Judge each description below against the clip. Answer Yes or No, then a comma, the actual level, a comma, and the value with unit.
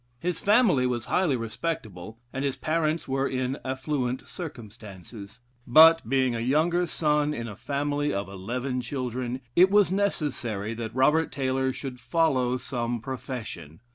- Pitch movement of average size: Yes, average, 4.2 semitones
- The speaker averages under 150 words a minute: Yes, average, 140 wpm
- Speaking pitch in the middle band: No, low, 130 Hz